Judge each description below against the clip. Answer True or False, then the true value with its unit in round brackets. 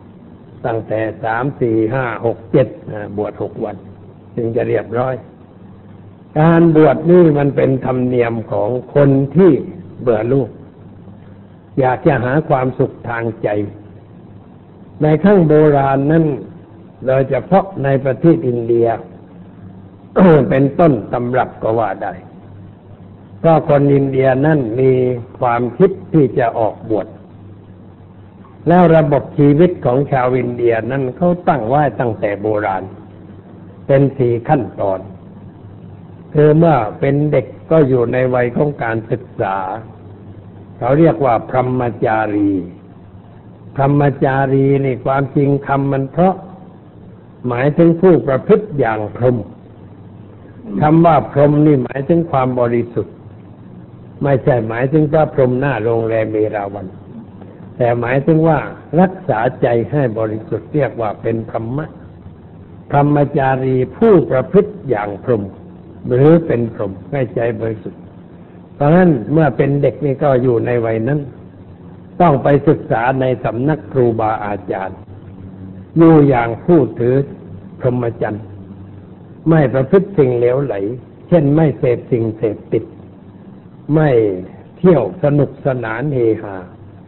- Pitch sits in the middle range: False (125 Hz)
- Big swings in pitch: True (5.8 semitones)